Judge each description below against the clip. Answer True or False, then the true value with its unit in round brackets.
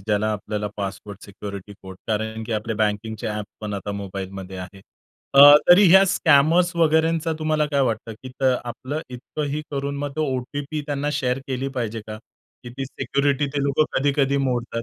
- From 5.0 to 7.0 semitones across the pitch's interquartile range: True (5.3 semitones)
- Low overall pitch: True (130 Hz)